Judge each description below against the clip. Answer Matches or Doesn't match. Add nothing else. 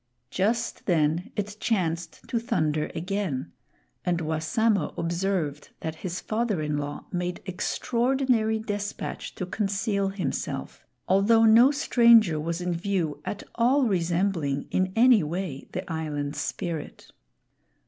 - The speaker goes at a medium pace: Doesn't match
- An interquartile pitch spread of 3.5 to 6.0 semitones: Matches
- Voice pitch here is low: Doesn't match